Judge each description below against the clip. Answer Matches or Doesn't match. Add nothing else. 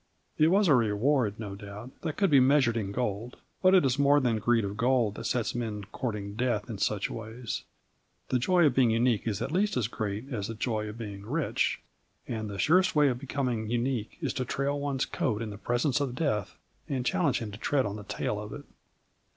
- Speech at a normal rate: Doesn't match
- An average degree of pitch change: Matches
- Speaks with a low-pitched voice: Matches